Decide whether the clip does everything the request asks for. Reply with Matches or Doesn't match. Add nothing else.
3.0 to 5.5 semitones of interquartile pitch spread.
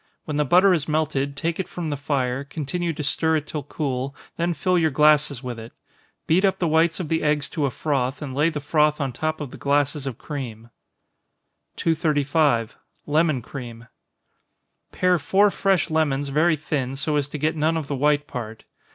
Doesn't match